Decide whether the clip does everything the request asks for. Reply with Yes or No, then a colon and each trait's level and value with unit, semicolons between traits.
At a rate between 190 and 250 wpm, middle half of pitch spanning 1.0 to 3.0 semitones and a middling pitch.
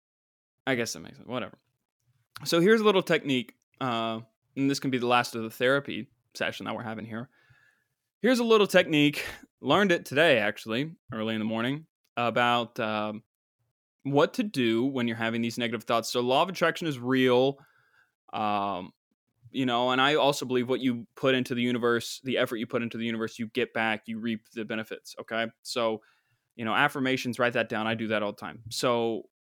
No: average, 200 wpm; average, 2.7 semitones; low, 120 Hz